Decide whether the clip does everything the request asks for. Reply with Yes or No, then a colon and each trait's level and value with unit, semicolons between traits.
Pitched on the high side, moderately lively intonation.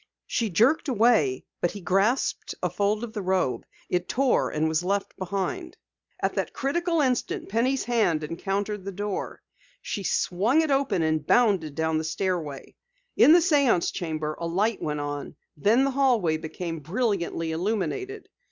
No: high, 195 Hz; wide, 6.8 semitones